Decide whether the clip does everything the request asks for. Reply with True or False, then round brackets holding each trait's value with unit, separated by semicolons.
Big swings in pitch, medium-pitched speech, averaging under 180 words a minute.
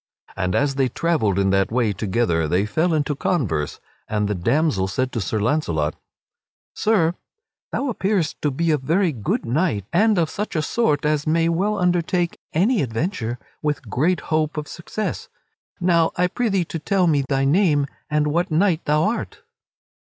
True (6.8 semitones; 155 Hz; 170 wpm)